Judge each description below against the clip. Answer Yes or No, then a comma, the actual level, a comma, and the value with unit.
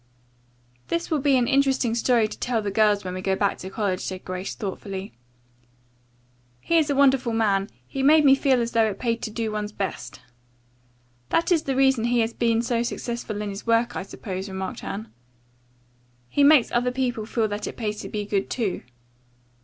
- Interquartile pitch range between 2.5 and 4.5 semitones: Yes, average, 4.1 semitones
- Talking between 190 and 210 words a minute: Yes, average, 195 wpm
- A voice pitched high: Yes, high, 230 Hz